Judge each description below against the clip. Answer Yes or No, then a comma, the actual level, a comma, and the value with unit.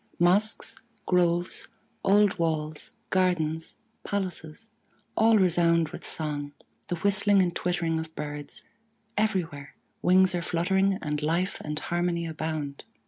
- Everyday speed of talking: No, slow, 115 wpm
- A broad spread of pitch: No, average, 3.1 semitones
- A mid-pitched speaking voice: Yes, medium, 175 Hz